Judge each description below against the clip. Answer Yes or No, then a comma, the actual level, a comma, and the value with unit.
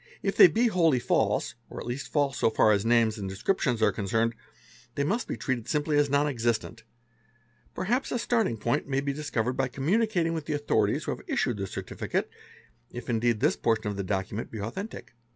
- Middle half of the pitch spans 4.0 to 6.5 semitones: Yes, average, 5.3 semitones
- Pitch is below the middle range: Yes, low, 125 Hz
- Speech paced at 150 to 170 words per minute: No, fast, 205 wpm